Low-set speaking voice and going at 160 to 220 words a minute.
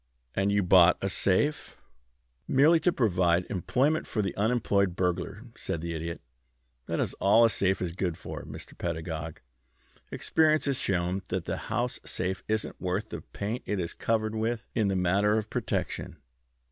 Yes: low, 100 Hz; average, 170 wpm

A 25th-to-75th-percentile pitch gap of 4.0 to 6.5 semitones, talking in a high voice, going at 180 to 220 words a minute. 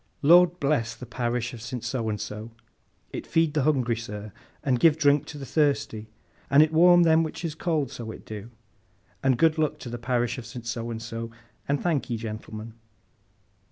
No: average, 4.9 semitones; low, 130 Hz; average, 190 wpm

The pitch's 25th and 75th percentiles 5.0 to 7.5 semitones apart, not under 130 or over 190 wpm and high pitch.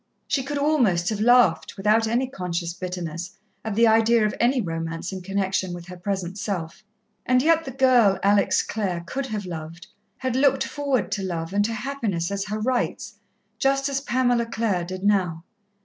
Yes: wide, 5.5 semitones; average, 180 wpm; high, 210 Hz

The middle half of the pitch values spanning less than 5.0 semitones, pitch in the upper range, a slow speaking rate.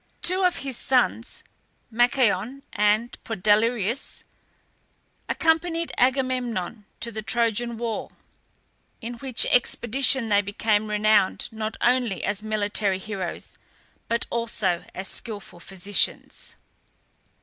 Yes: average, 3.1 semitones; high, 225 Hz; slow, 100 wpm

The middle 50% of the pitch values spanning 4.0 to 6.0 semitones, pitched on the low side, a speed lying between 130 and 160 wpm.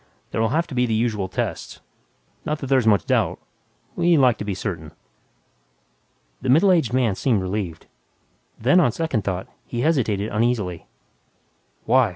Yes: average, 4.6 semitones; low, 115 Hz; average, 155 wpm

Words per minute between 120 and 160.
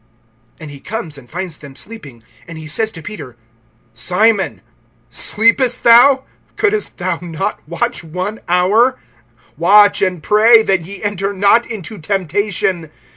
Yes: slow, 135 wpm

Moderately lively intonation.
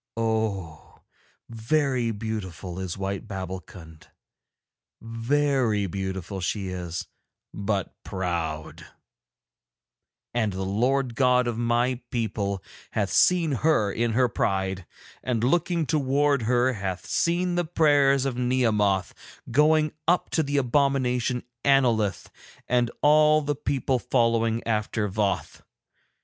No: wide, 5.7 semitones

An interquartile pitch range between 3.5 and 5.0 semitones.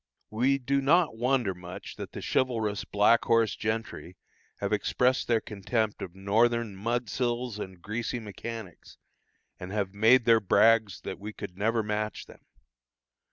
No: average, 2.8 semitones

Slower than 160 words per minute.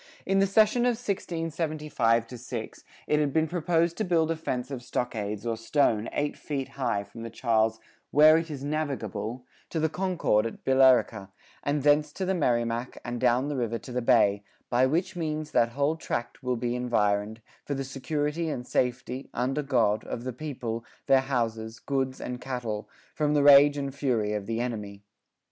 No: average, 185 wpm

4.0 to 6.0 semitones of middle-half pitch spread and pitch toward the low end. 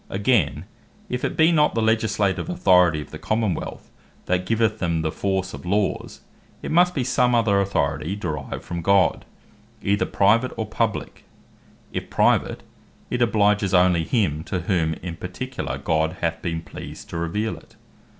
Yes: average, 4.9 semitones; low, 100 Hz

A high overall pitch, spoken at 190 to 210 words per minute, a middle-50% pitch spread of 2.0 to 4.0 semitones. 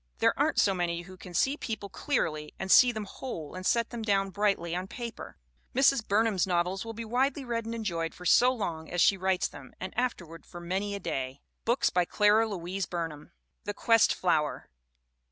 No: high, 195 Hz; average, 195 wpm; average, 4.7 semitones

